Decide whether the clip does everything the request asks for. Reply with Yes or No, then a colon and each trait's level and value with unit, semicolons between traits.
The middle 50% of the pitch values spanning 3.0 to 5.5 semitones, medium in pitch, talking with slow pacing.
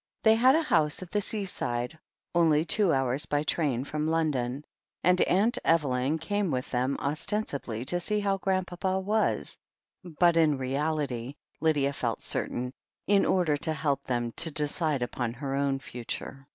No: average, 5.1 semitones; medium, 150 Hz; average, 155 wpm